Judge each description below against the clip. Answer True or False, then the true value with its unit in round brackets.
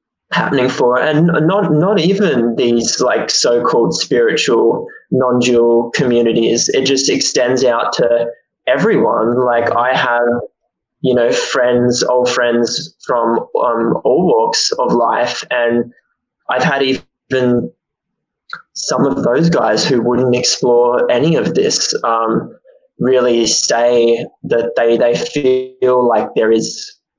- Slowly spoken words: True (125 wpm)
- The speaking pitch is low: True (125 Hz)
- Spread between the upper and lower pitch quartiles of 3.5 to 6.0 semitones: True (4.7 semitones)